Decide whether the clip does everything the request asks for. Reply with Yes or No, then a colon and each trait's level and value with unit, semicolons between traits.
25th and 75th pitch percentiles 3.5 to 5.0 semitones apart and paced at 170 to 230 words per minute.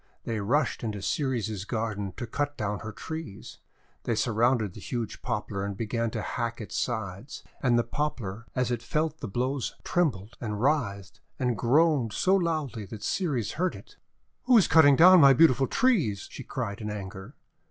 No: wide, 5.5 semitones; average, 175 wpm